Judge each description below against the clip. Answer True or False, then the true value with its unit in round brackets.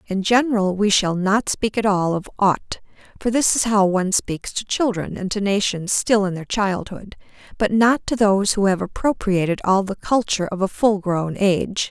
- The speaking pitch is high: True (200 Hz)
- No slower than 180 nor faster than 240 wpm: True (200 wpm)